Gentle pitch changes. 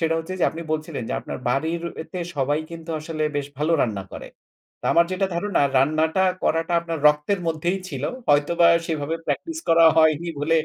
Yes: narrow, 2.2 semitones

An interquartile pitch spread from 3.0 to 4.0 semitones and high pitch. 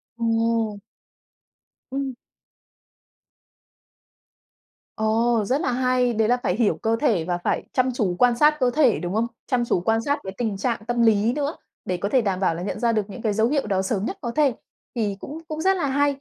Yes: average, 3.6 semitones; high, 230 Hz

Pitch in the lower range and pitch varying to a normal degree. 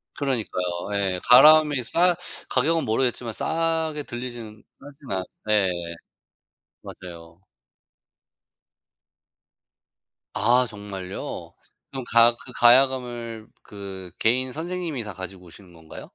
No: low, 120 Hz; wide, 5.7 semitones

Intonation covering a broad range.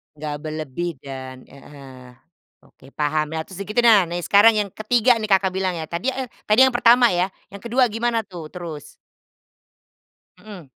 Yes: wide, 6.4 semitones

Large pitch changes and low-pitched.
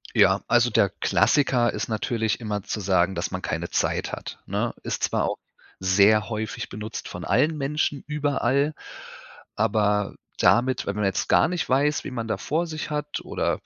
Yes: wide, 5.7 semitones; low, 115 Hz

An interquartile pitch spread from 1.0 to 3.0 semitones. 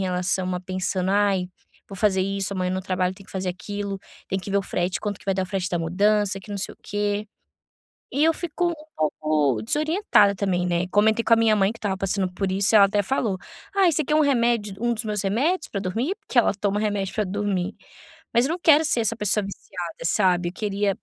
Yes: average, 2.7 semitones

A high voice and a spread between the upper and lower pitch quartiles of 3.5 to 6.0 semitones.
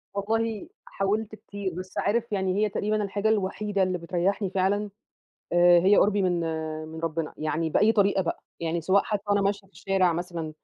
No: high, 195 Hz; average, 3.0 semitones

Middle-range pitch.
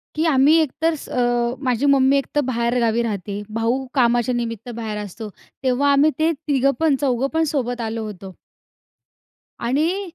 No: very high, 250 Hz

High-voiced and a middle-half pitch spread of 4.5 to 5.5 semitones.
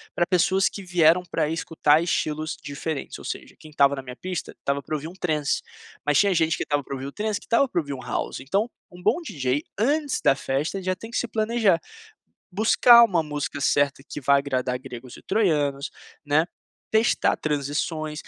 No: medium, 155 Hz; average, 5.1 semitones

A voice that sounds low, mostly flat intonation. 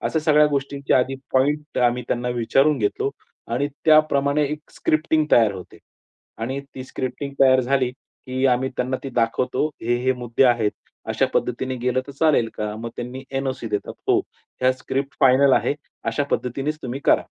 Yes: low, 130 Hz; narrow, 2.3 semitones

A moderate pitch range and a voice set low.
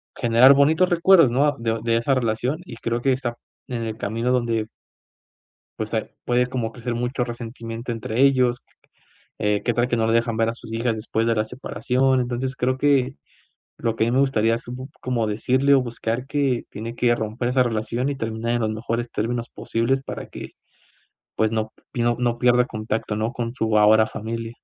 No: narrow, 2.0 semitones; low, 120 Hz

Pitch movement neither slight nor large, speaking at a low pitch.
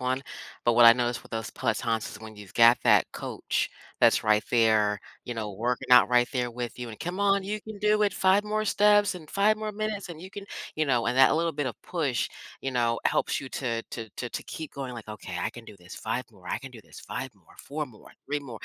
No: wide, 7.8 semitones; low, 125 Hz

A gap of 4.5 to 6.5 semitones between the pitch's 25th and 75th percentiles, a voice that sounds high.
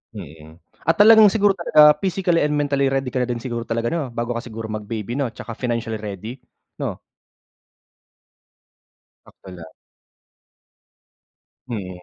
No: average, 5.2 semitones; low, 120 Hz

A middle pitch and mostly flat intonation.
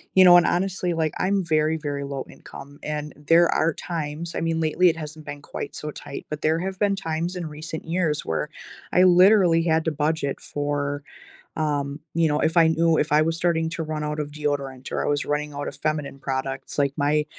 Yes: medium, 155 Hz; narrow, 2.3 semitones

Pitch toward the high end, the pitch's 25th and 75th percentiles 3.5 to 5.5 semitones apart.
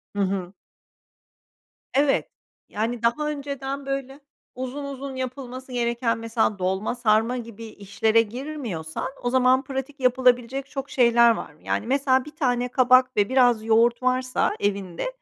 No: very high, 250 Hz; average, 2.9 semitones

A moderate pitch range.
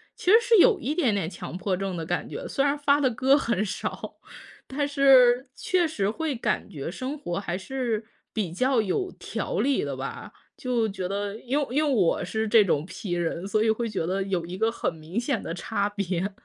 No: wide, 6.3 semitones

